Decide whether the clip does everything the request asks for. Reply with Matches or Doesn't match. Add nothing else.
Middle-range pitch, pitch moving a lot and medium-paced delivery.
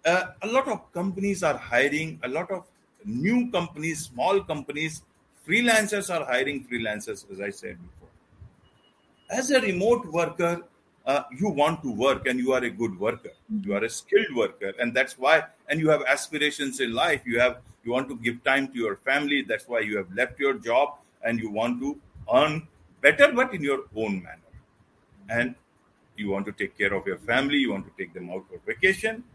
Matches